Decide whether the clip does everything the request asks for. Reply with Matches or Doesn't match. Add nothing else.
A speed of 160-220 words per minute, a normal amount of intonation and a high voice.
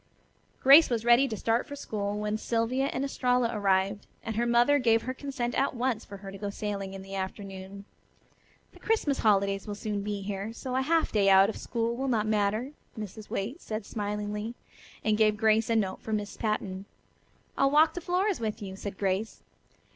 Matches